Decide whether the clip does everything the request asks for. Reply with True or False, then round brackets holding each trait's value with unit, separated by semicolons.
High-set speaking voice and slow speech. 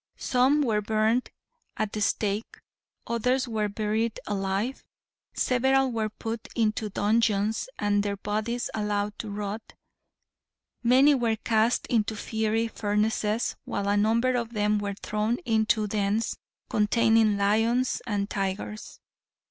True (215 Hz; 125 wpm)